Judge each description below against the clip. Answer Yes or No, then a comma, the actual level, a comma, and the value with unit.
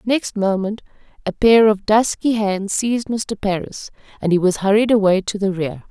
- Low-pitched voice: No, high, 205 Hz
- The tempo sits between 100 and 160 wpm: No, average, 185 wpm